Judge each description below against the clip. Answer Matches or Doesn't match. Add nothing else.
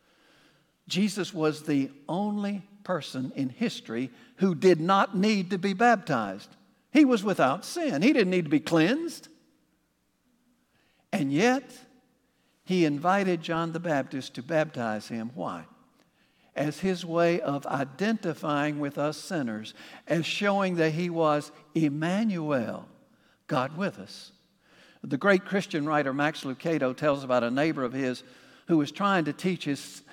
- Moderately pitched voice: Matches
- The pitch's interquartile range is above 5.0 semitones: Matches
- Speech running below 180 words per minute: Matches